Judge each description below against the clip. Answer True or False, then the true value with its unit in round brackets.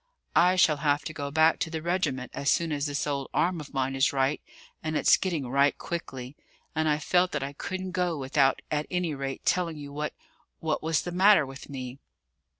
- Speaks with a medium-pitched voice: True (150 Hz)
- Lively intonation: False (3.3 semitones)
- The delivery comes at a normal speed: False (210 wpm)